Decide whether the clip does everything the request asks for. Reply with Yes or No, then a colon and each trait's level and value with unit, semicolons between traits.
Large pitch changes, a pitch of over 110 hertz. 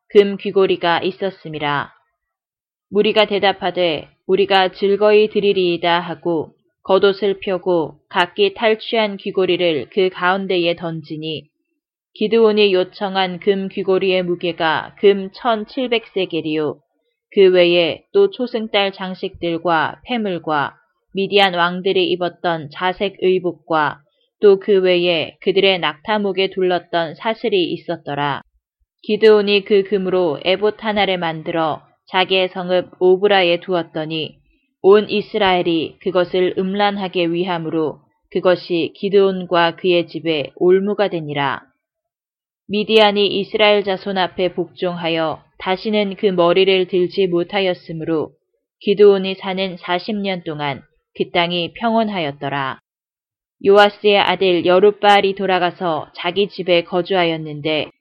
No: average, 2.9 semitones; medium, 185 Hz